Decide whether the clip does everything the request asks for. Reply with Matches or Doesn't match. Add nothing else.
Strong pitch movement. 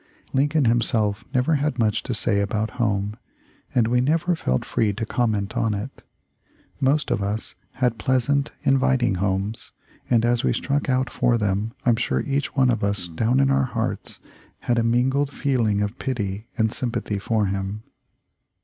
Doesn't match